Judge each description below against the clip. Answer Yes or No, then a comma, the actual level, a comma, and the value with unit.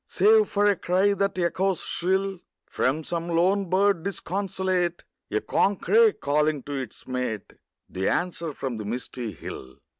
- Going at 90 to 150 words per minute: Yes, average, 145 wpm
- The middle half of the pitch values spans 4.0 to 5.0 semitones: No, wide, 5.6 semitones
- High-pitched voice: No, medium, 175 Hz